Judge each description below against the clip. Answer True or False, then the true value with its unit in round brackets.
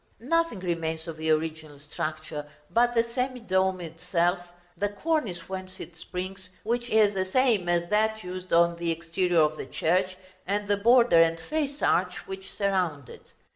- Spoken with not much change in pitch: False (4.3 semitones)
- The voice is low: False (185 Hz)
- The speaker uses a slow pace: False (170 wpm)